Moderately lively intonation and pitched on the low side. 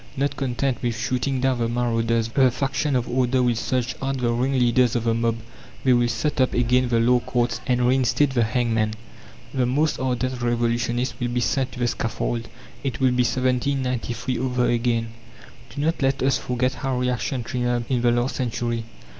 No: narrow, 1.6 semitones; low, 125 Hz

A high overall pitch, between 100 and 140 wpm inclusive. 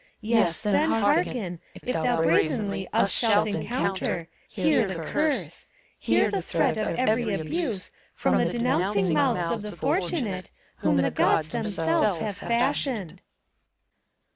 Yes: high, 210 Hz; slow, 135 wpm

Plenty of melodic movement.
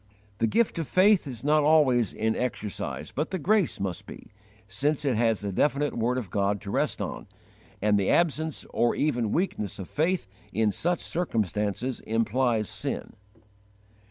Yes: wide, 6.3 semitones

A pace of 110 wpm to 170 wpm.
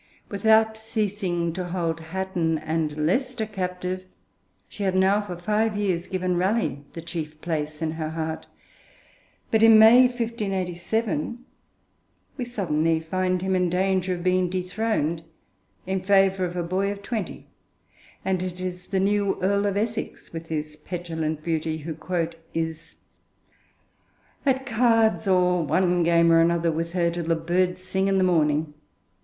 Yes: average, 150 wpm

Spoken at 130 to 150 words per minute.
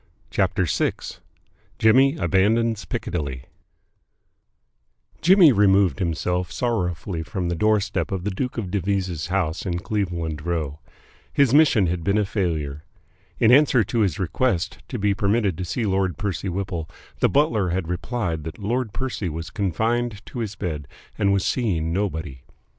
Yes: average, 145 wpm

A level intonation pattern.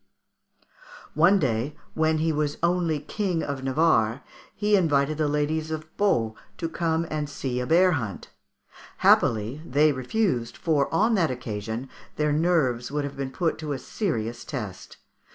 No: average, 4.2 semitones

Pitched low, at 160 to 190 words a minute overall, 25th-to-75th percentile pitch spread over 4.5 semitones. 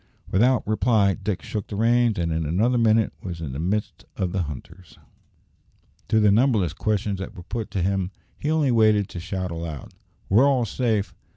No: low, 100 Hz; average, 185 wpm; average, 4.0 semitones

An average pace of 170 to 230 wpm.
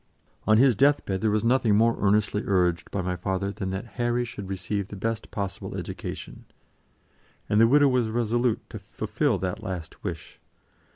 Yes: average, 175 wpm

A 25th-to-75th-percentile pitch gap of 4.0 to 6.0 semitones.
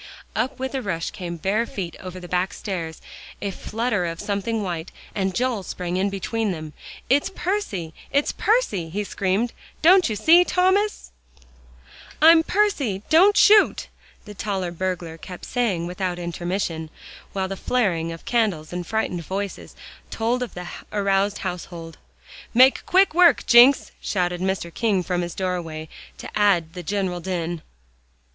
Yes: average, 5.3 semitones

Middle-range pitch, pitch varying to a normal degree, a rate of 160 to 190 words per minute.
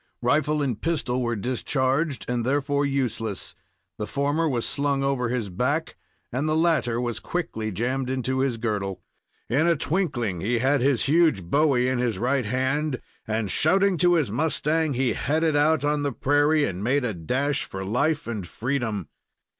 No: low, 130 Hz; average, 4.0 semitones; average, 170 wpm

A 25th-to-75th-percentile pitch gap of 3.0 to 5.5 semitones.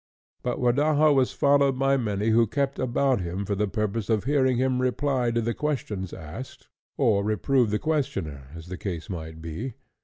Yes: average, 5.2 semitones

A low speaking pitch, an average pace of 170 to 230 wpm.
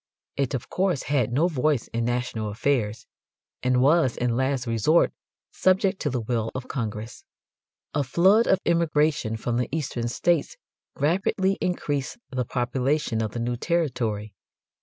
No: low, 130 Hz; average, 145 wpm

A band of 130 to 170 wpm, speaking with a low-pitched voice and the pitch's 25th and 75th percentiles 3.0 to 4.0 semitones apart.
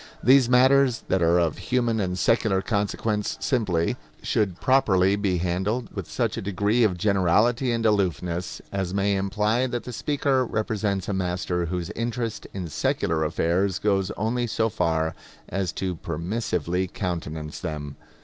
No: average, 150 wpm; low, 100 Hz; average, 4.4 semitones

